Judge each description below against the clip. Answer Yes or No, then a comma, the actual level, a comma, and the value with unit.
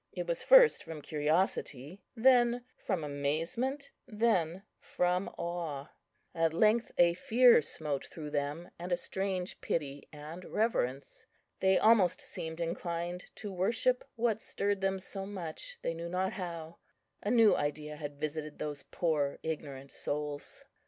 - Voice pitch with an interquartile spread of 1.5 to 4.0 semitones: No, average, 5.3 semitones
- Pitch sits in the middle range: Yes, medium, 170 Hz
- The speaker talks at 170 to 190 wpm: No, average, 140 wpm